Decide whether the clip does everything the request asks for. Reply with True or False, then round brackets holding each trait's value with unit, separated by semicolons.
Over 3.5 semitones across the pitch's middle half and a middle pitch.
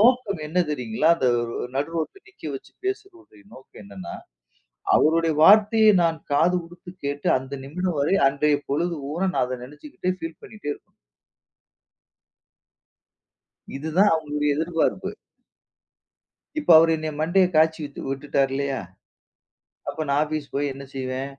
True (4.0 semitones; 155 Hz)